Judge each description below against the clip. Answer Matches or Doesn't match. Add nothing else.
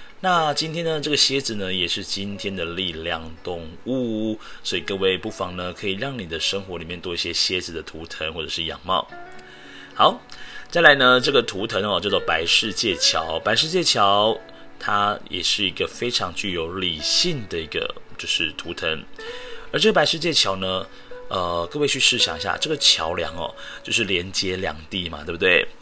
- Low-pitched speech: Matches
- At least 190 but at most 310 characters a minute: Matches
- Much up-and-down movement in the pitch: Matches